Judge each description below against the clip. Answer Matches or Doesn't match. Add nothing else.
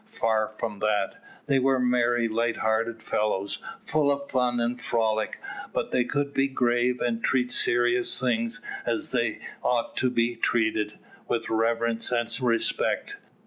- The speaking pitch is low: Matches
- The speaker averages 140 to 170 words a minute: Matches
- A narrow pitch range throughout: Matches